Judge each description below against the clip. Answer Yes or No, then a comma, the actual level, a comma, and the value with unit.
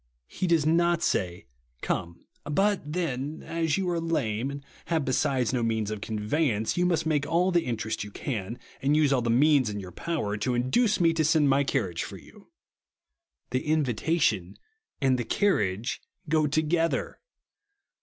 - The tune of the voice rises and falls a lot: Yes, wide, 6.6 semitones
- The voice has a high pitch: No, medium, 140 Hz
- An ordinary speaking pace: Yes, average, 165 wpm